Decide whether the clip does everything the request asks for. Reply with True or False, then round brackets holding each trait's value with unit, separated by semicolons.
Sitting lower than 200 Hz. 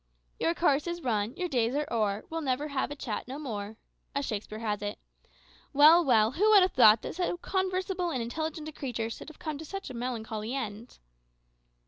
False (270 Hz)